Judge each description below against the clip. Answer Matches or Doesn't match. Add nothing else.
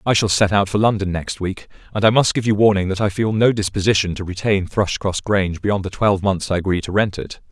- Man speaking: Matches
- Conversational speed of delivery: Doesn't match